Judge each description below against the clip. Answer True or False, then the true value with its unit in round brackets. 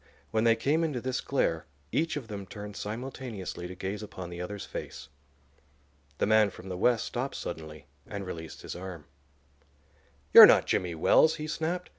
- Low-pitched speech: True (105 Hz)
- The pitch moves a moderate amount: False (6.2 semitones)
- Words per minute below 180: True (170 wpm)